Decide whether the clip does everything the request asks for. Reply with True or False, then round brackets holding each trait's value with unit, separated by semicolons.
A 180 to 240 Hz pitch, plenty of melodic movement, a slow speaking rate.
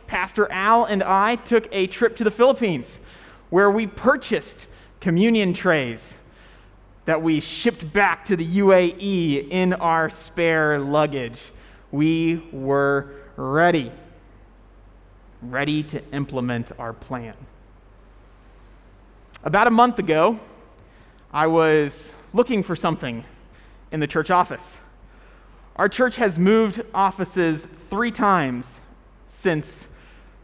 False (165 Hz; 6.4 semitones; 110 wpm)